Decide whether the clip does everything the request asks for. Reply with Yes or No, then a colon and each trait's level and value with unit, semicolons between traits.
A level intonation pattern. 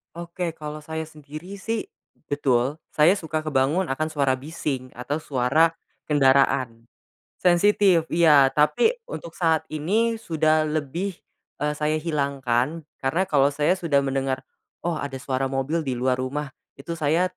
No: average, 3.5 semitones